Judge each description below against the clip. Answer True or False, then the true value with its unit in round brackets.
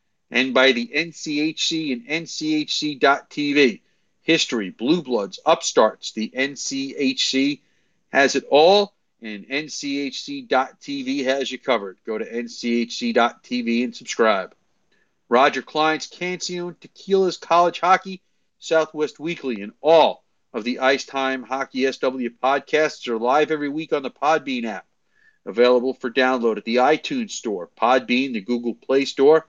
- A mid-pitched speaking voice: True (145 Hz)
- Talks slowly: True (125 wpm)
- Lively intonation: True (6.1 semitones)